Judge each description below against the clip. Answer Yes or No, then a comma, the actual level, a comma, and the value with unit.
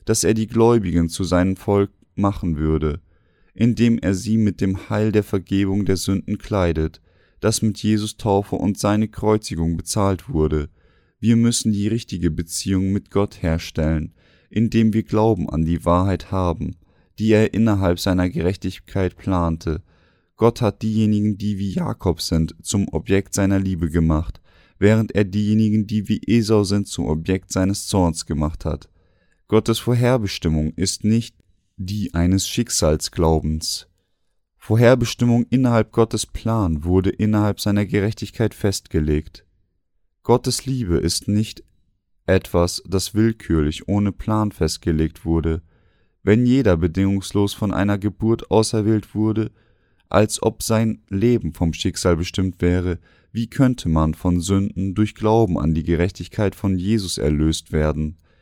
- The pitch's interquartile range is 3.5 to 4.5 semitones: Yes, average, 3.9 semitones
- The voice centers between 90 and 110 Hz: Yes, very low, 95 Hz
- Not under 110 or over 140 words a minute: Yes, average, 135 wpm